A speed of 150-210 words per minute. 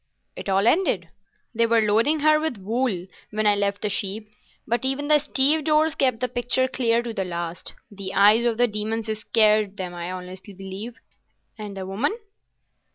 Yes: average, 175 wpm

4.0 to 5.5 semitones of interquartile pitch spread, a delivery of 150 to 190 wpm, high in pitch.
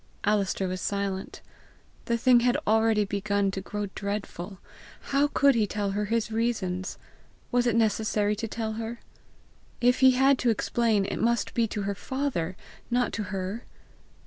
No: average, 3.0 semitones; average, 160 wpm; high, 215 Hz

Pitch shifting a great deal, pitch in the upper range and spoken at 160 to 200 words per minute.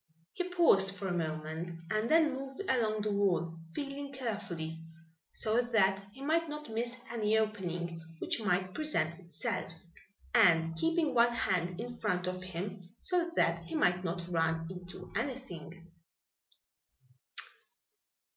No: wide, 6.1 semitones; high, 200 Hz; slow, 135 wpm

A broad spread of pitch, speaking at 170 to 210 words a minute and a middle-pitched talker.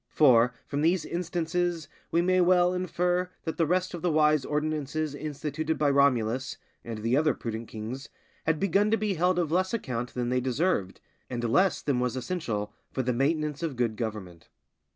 Yes: wide, 6.0 semitones; average, 180 wpm; medium, 150 Hz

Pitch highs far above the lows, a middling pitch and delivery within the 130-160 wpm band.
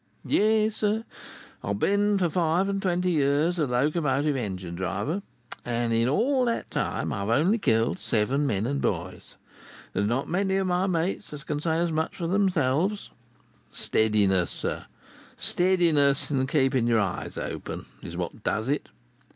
Yes: wide, 7.9 semitones; medium, 150 Hz; average, 155 wpm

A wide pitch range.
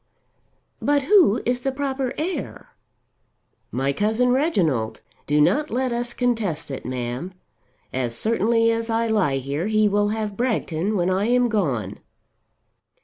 Yes: wide, 7.8 semitones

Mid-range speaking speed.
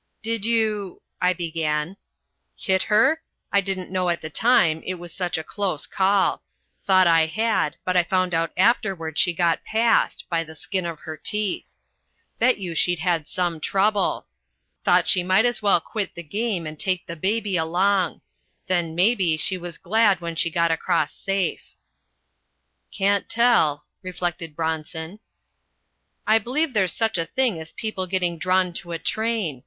Yes: average, 165 wpm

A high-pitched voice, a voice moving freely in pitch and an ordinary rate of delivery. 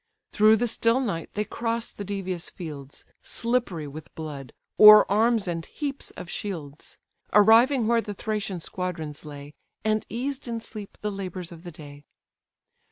Yes: high, 200 Hz; wide, 5.7 semitones; average, 155 wpm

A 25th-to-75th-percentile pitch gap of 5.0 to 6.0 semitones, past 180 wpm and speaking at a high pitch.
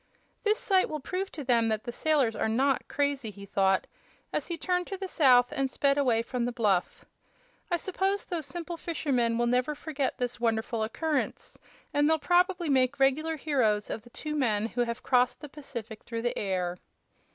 Yes: average, 5.3 semitones; average, 190 wpm; very high, 265 Hz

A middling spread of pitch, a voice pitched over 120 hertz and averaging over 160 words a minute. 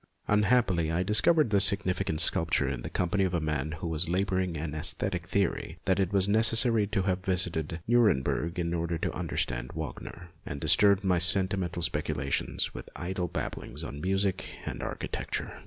No: average, 3.2 semitones; very low, 90 Hz; average, 170 wpm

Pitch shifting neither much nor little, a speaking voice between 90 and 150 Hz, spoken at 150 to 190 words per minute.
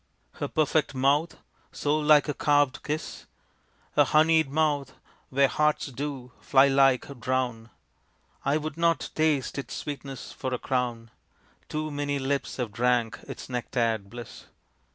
No: average, 3.1 semitones; medium, 140 Hz; slow, 135 wpm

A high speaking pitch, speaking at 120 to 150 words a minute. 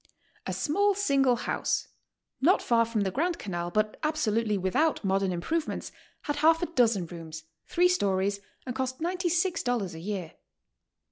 Yes: high, 245 Hz; average, 145 wpm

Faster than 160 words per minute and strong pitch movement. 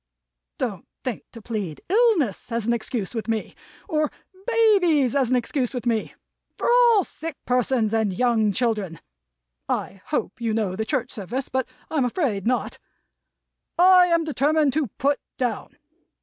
No: average, 150 wpm; wide, 5.7 semitones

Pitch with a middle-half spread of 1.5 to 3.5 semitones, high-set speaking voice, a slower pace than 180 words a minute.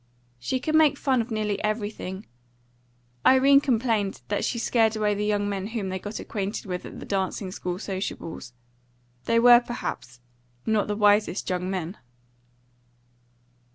Yes: average, 3.2 semitones; high, 210 Hz; average, 150 wpm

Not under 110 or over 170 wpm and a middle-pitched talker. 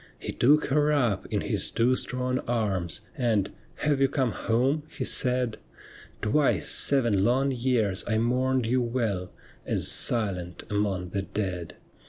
No: average, 160 wpm; low, 120 Hz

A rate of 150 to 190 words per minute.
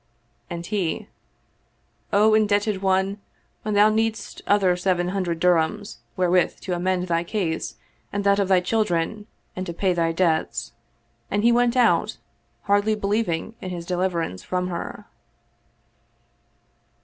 No: slow, 135 wpm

